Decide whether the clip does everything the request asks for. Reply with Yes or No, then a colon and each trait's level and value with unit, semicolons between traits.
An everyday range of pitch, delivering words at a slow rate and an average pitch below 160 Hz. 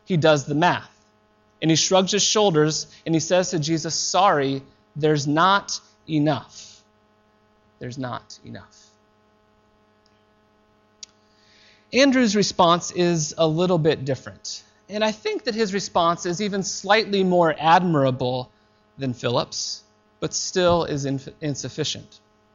No: wide, 8.5 semitones; slow, 120 wpm; low, 135 Hz